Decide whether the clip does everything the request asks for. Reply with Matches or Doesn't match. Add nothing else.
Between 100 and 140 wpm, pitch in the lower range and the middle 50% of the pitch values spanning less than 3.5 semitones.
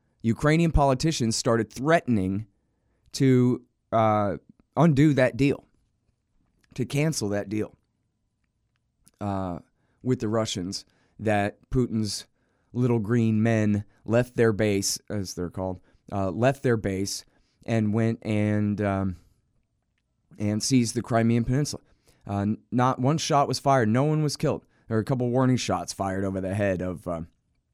Doesn't match